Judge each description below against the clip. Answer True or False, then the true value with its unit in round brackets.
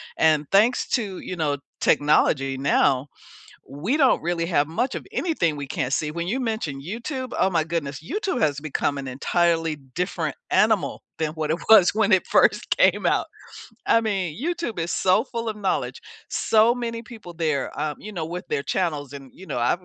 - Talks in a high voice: False (170 Hz)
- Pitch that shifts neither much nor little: False (7.0 semitones)